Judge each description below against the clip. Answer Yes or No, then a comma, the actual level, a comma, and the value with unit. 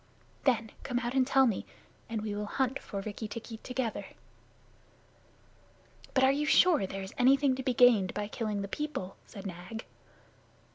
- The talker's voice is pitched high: Yes, high, 230 Hz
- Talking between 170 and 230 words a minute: Yes, average, 175 wpm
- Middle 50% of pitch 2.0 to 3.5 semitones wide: No, average, 4.3 semitones